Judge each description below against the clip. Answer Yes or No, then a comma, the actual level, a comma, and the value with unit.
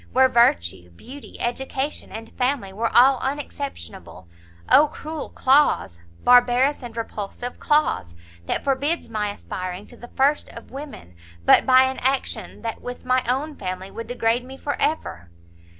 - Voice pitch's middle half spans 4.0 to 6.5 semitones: Yes, average, 4.7 semitones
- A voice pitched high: Yes, high, 245 Hz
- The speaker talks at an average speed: Yes, average, 150 wpm